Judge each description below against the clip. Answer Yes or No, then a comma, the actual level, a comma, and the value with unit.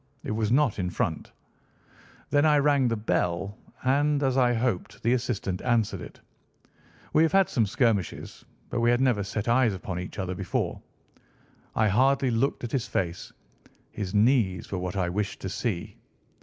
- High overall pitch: No, low, 115 Hz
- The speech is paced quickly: No, average, 170 wpm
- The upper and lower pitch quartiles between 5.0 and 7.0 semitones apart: Yes, average, 5.3 semitones